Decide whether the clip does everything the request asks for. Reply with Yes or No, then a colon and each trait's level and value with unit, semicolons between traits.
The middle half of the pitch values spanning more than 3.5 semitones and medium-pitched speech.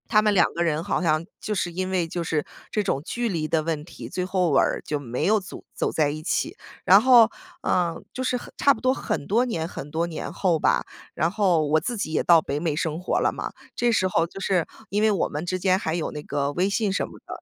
Yes: average, 4.2 semitones; medium, 175 Hz